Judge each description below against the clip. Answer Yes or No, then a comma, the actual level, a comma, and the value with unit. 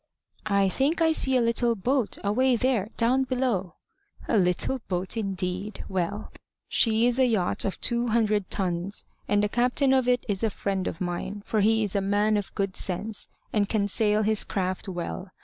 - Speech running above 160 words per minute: Yes, average, 185 wpm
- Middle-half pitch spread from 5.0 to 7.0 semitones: No, average, 3.7 semitones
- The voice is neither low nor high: No, high, 210 Hz